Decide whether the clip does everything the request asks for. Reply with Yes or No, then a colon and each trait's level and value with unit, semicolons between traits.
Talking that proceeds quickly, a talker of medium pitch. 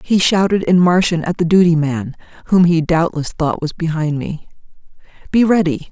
No: average, 170 wpm; medium, 170 Hz